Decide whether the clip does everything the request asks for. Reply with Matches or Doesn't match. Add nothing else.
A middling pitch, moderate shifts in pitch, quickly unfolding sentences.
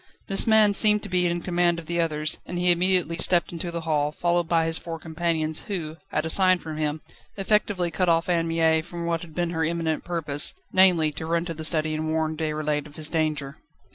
Doesn't match